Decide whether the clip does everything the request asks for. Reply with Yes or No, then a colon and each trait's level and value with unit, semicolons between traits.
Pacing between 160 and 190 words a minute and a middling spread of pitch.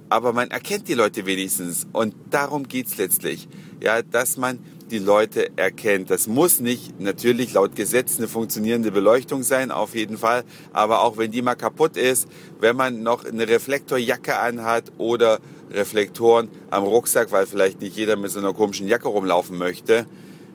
Yes: average, 170 wpm; average, 3.3 semitones